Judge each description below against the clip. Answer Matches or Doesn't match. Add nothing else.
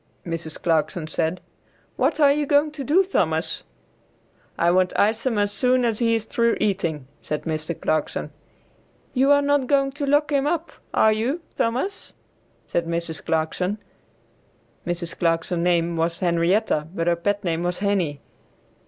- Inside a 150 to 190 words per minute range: Matches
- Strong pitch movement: Matches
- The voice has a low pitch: Doesn't match